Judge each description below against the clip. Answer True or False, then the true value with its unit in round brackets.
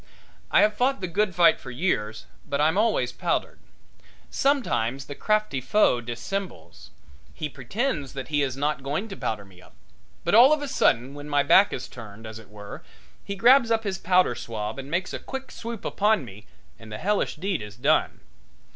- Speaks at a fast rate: False (190 wpm)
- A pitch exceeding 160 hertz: False (150 Hz)